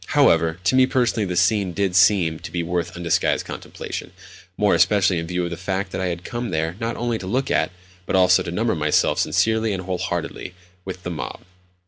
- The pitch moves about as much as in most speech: Yes, average, 3.2 semitones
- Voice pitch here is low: Yes, very low, 90 Hz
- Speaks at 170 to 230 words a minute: Yes, average, 200 wpm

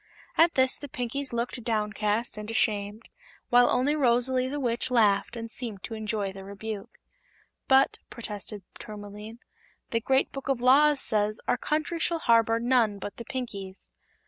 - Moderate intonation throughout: Yes, average, 3.5 semitones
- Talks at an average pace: Yes, average, 155 wpm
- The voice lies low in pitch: No, high, 230 Hz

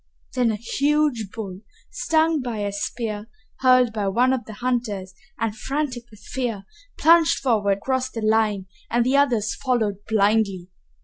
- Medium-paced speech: Yes, average, 150 wpm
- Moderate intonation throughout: Yes, average, 3.7 semitones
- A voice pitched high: Yes, high, 230 Hz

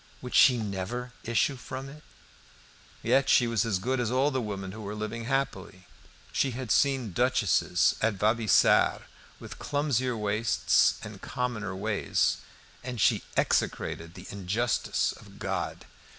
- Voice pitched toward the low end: Yes, low, 115 Hz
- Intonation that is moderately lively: Yes, average, 3.8 semitones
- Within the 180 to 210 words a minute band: No, average, 140 wpm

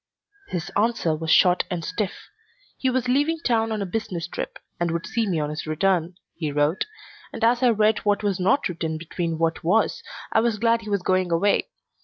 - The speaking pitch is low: No, high, 190 Hz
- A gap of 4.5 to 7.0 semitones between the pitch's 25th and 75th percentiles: Yes, average, 5.1 semitones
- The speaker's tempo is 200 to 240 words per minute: Yes, fast, 205 wpm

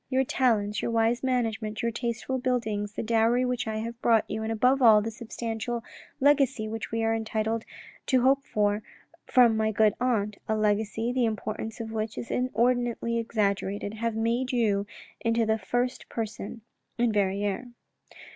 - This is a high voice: Yes, high, 225 Hz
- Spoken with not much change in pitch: Yes, narrow, 2.0 semitones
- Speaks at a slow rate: No, average, 165 wpm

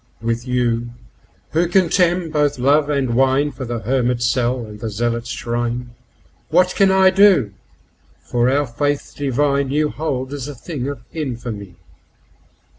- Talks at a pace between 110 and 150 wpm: Yes, average, 140 wpm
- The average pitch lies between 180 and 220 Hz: No, low, 130 Hz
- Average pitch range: Yes, average, 3.7 semitones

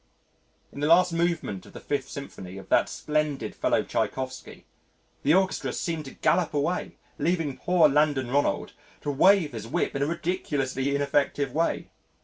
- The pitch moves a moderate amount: Yes, average, 3.5 semitones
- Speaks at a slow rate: No, average, 155 wpm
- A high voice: No, medium, 145 Hz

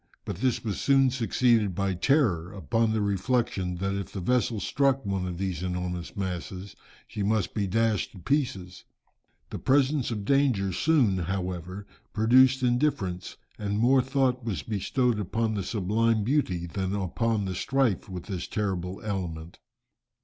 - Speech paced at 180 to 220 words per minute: No, average, 150 wpm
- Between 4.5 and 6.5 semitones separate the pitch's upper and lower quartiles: Yes, average, 4.9 semitones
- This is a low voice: Yes, low, 105 Hz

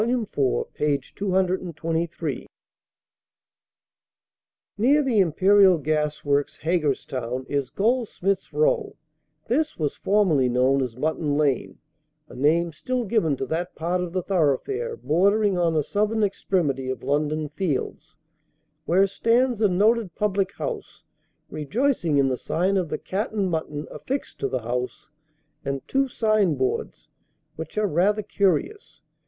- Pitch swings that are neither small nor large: No, wide, 6.2 semitones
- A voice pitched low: No, medium, 175 Hz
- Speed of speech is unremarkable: No, slow, 130 wpm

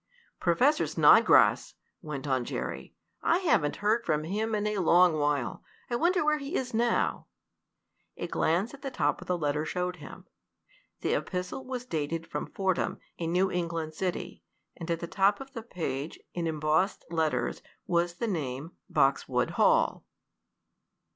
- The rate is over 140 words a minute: Yes, average, 155 wpm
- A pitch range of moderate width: No, wide, 5.9 semitones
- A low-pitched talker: No, medium, 175 Hz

